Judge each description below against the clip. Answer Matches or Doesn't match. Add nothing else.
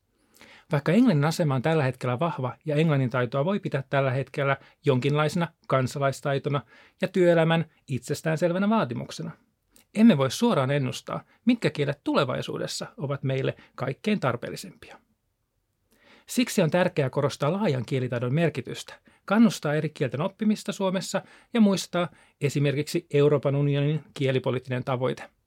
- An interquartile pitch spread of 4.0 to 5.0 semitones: Matches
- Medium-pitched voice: Matches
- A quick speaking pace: Doesn't match